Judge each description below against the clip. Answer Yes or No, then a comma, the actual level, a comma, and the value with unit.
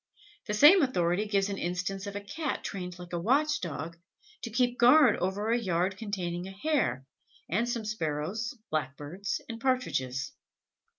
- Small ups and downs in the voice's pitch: No, average, 5.3 semitones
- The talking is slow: No, average, 160 wpm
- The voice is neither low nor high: No, high, 200 Hz